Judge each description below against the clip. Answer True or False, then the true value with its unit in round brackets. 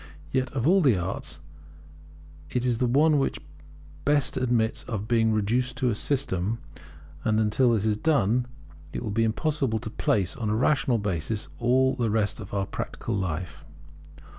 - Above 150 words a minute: True (165 wpm)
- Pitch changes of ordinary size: True (3.7 semitones)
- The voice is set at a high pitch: False (115 Hz)